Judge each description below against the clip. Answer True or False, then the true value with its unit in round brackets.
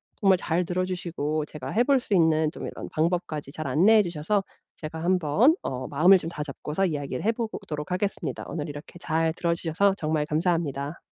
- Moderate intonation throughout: True (3.6 semitones)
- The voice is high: False (165 Hz)